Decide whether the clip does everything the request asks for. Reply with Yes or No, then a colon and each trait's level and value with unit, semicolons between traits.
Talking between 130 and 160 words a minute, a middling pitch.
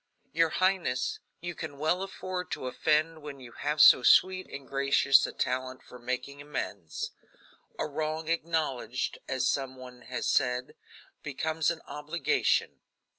Yes: average, 140 wpm; medium, 145 Hz